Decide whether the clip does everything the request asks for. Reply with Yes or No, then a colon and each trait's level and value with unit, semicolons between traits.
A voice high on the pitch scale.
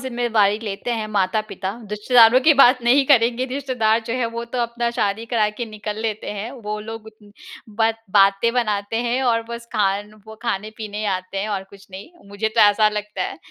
Yes: high, 220 Hz